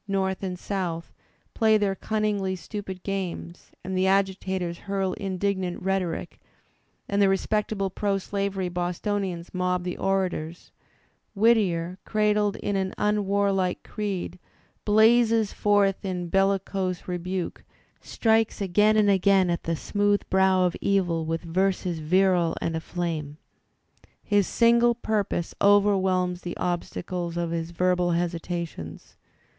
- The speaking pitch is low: No, high, 190 Hz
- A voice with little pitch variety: Yes, narrow, 2.3 semitones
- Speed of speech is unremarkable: No, slow, 120 wpm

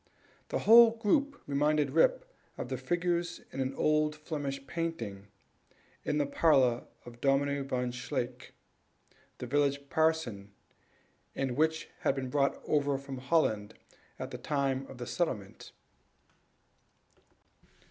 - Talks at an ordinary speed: No, slow, 120 wpm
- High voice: No, medium, 140 Hz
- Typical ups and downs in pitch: Yes, average, 3.7 semitones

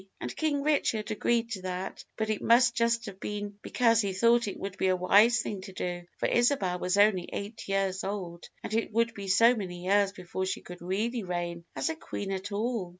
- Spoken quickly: Yes, fast, 215 wpm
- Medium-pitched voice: No, high, 205 Hz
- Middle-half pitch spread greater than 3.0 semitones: Yes, average, 3.7 semitones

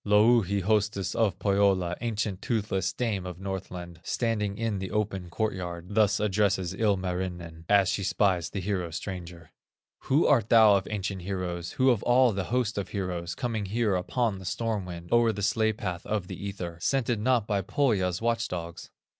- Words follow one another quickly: No, average, 175 wpm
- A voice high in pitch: No, low, 100 Hz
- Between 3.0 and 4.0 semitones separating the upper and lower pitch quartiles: Yes, average, 3.3 semitones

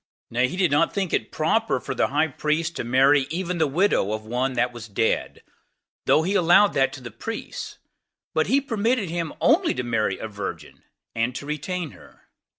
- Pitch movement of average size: No, wide, 6.8 semitones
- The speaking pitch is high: No, medium, 145 Hz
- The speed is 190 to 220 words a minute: Yes, average, 195 wpm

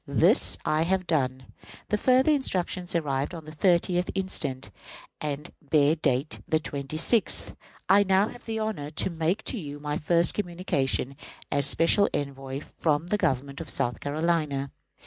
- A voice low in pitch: No, medium, 155 Hz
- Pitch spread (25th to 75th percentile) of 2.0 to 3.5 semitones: No, average, 4.6 semitones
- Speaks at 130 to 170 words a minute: Yes, average, 150 wpm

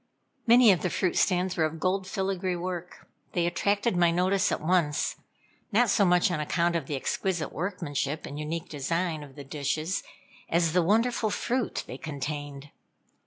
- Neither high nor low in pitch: Yes, medium, 175 Hz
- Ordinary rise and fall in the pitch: Yes, average, 3.6 semitones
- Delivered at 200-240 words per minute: No, average, 165 wpm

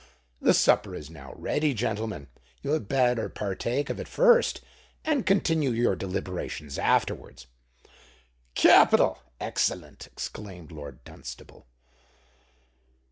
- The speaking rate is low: Yes, slow, 100 wpm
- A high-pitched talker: No, low, 110 Hz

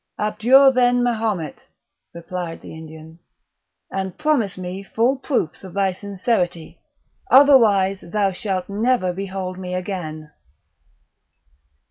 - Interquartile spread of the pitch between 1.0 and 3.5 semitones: No, average, 4.1 semitones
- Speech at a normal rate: No, slow, 105 wpm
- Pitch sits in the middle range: No, high, 195 Hz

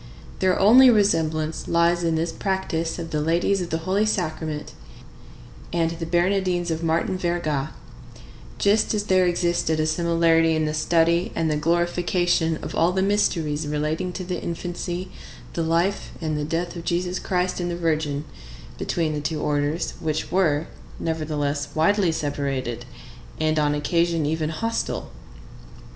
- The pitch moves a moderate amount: No, narrow, 2.3 semitones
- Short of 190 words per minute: Yes, average, 150 wpm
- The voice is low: No, medium, 165 Hz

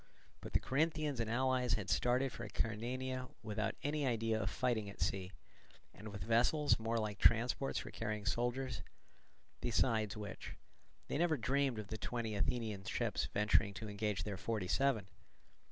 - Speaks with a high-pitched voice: No, low, 115 Hz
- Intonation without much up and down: No, average, 3.3 semitones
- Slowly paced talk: No, average, 155 wpm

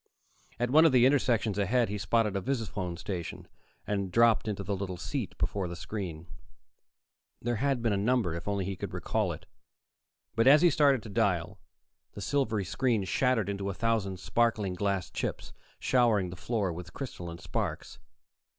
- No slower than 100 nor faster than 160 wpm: No, average, 175 wpm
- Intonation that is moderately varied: Yes, average, 4.2 semitones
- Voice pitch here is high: No, low, 105 Hz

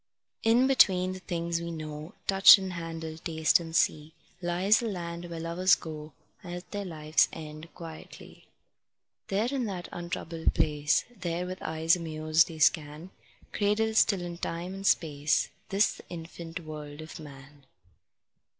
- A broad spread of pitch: No, average, 2.8 semitones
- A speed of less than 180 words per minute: Yes, average, 150 wpm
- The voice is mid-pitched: Yes, medium, 170 Hz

